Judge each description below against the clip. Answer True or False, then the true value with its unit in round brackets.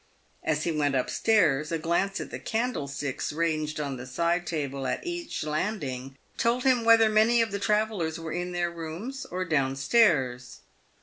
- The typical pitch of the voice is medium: True (165 Hz)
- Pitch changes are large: True (6.9 semitones)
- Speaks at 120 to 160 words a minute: False (175 wpm)